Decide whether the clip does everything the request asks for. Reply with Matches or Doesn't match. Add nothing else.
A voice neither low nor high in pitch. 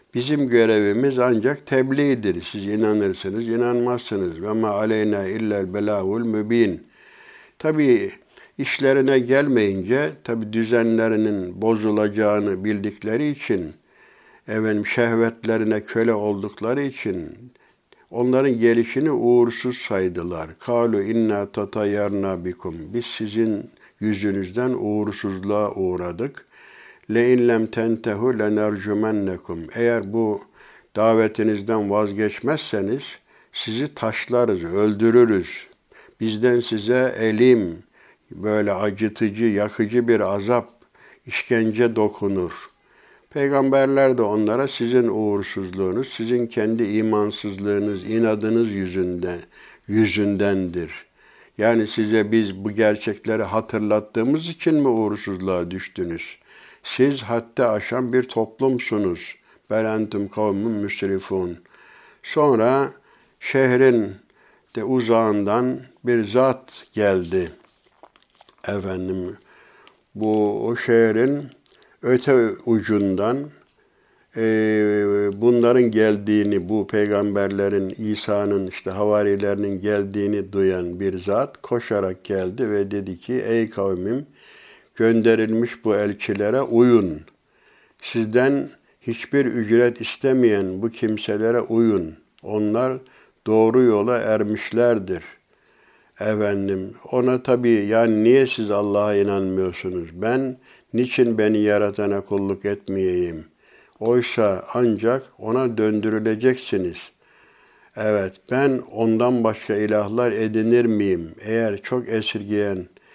Doesn't match